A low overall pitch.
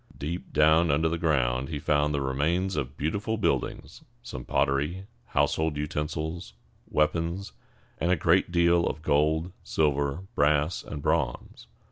Yes: very low, 75 Hz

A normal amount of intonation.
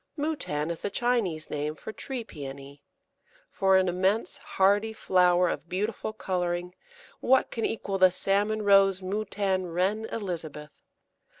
Yes: average, 3.5 semitones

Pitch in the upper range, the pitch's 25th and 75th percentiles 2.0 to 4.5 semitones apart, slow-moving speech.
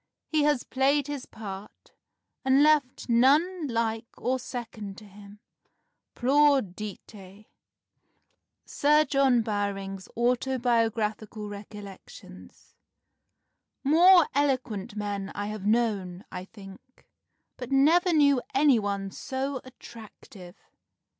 No: high, 235 Hz; average, 5.1 semitones; slow, 100 wpm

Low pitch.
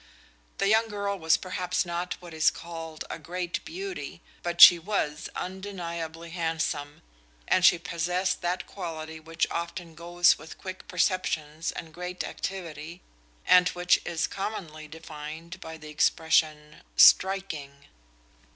No: medium, 170 Hz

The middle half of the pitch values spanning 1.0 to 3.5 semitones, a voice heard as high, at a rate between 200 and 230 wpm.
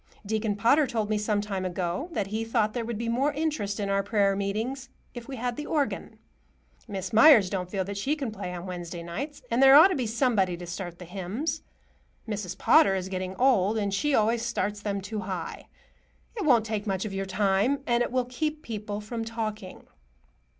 No: average, 4.0 semitones; high, 215 Hz; fast, 205 wpm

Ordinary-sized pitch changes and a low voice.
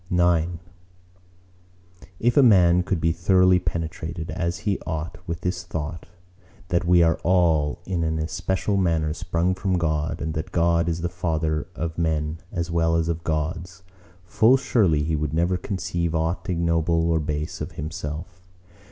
No: narrow, 2.0 semitones; very low, 85 Hz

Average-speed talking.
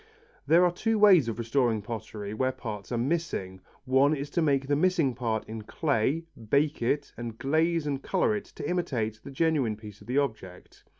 Yes: average, 190 wpm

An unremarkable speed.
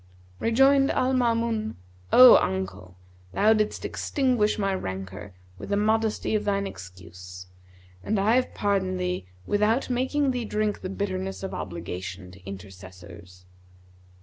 No: slow, 130 wpm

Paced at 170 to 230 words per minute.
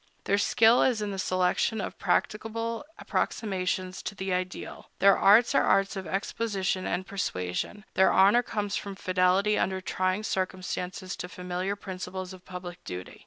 No: average, 155 wpm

